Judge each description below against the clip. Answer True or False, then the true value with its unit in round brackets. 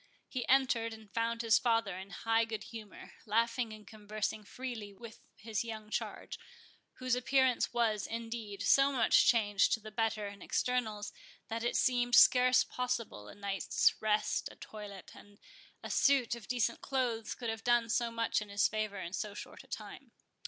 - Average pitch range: False (2.3 semitones)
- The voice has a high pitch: True (225 Hz)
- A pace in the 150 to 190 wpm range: True (175 wpm)